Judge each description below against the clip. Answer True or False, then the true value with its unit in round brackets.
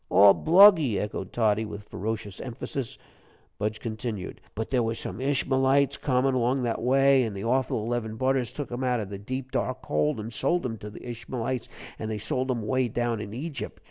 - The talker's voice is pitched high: False (120 Hz)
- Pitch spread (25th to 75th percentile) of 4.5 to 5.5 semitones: False (3.4 semitones)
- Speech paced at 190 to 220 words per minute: True (195 wpm)